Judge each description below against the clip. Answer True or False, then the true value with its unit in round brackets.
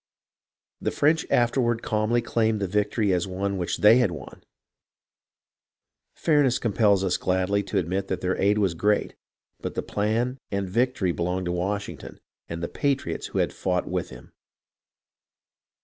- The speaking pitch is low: True (100 Hz)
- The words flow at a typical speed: True (150 wpm)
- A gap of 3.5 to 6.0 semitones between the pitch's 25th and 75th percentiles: True (4.0 semitones)